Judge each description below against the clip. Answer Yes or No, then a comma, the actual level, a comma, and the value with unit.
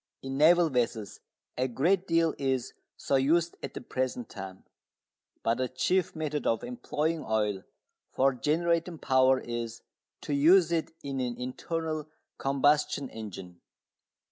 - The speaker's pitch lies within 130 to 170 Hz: Yes, low, 135 Hz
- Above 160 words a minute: No, slow, 135 wpm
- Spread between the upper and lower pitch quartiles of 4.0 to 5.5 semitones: Yes, average, 4.8 semitones